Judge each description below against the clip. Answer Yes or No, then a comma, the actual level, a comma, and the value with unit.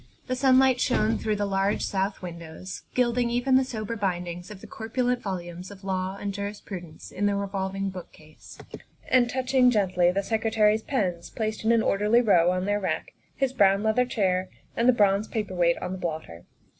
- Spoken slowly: No, average, 190 wpm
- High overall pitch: Yes, high, 200 Hz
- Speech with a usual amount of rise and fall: Yes, average, 3.9 semitones